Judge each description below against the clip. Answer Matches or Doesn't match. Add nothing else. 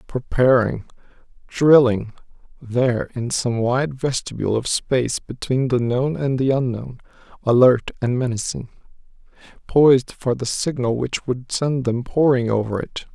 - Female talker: Doesn't match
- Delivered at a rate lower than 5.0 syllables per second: Matches